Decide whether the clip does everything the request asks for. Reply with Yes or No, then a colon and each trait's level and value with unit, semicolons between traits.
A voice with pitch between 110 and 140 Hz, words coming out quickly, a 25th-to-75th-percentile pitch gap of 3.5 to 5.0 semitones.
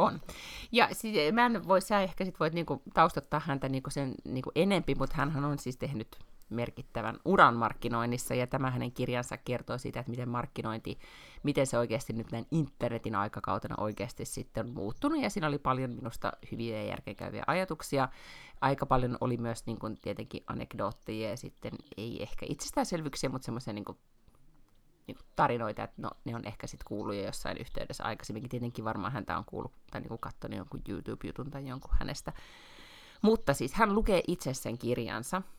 Yes: low, 130 Hz; fast, 170 wpm; average, 4.1 semitones